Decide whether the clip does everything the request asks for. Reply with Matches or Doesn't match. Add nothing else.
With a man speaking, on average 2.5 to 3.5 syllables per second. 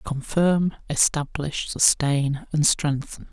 Matches